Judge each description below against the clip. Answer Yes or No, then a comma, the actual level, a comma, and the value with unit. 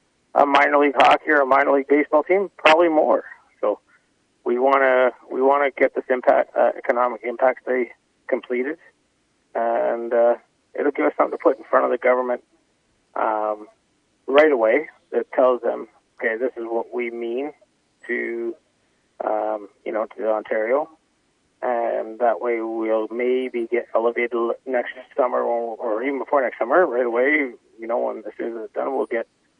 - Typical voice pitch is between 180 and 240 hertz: No, low, 120 Hz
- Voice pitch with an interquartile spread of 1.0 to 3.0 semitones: Yes, narrow, 2.6 semitones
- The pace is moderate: Yes, average, 160 wpm